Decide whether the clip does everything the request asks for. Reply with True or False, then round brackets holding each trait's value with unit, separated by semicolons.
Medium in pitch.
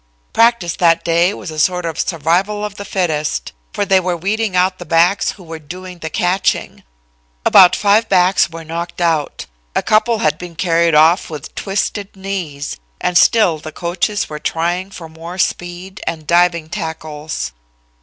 True (175 Hz)